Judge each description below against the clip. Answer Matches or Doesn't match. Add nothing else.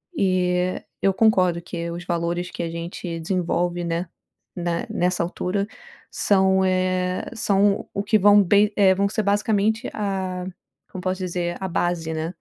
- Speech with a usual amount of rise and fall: Doesn't match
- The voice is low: Doesn't match